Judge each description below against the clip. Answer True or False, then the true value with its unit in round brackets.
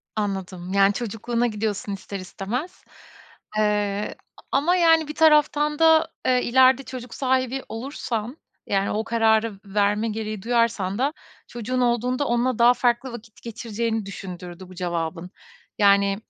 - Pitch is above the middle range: True (225 Hz)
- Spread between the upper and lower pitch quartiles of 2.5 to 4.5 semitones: True (4.1 semitones)